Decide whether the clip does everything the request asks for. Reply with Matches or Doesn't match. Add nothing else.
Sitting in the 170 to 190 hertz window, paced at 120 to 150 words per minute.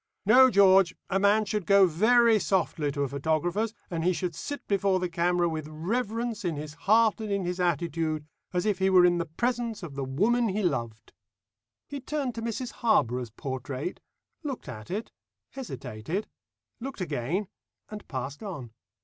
Doesn't match